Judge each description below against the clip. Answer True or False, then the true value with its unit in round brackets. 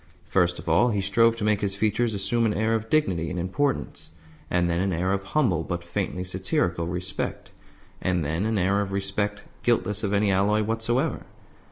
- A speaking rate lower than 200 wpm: True (190 wpm)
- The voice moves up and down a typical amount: True (3.4 semitones)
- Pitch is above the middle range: False (100 Hz)